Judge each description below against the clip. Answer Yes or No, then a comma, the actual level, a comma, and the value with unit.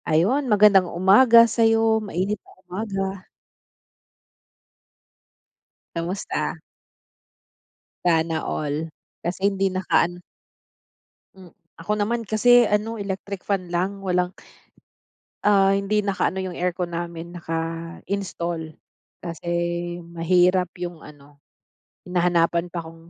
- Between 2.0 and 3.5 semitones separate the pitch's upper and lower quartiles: Yes, average, 2.9 semitones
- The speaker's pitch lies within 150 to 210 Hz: Yes, medium, 185 Hz